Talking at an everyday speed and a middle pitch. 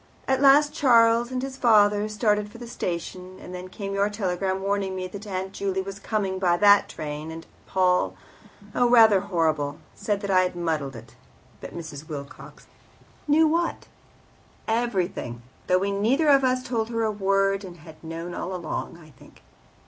No: average, 180 wpm; high, 195 Hz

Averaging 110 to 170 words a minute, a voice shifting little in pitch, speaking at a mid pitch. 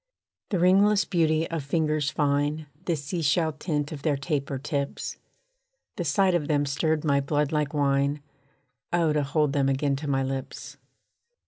Yes: average, 160 wpm; narrow, 2.2 semitones; medium, 150 Hz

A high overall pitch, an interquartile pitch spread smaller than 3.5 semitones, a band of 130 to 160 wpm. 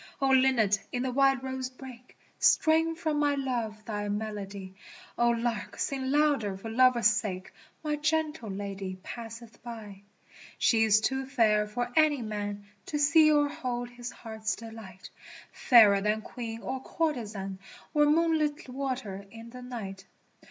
No: high, 240 Hz; average, 4.3 semitones; average, 155 wpm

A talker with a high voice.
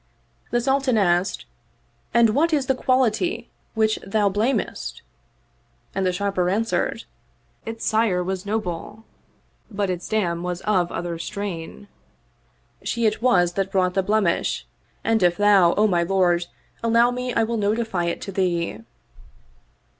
Yes: high, 200 Hz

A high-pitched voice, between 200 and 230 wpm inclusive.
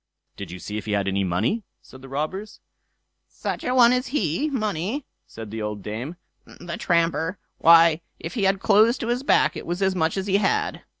No: medium, 170 Hz; fast, 205 wpm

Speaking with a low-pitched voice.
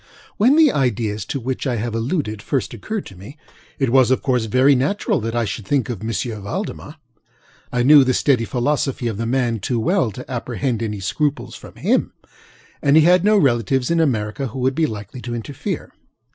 Yes: low, 125 Hz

